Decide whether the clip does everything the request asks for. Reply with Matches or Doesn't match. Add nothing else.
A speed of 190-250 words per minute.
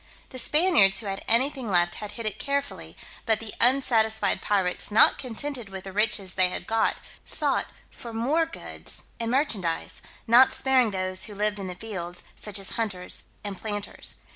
Doesn't match